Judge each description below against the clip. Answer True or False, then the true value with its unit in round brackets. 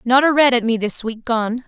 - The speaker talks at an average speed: False (285 wpm)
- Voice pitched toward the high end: True (240 Hz)